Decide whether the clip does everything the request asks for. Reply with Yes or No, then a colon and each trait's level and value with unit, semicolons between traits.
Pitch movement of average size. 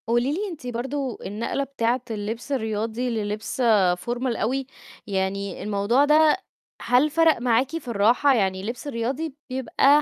Yes: average, 4.0 semitones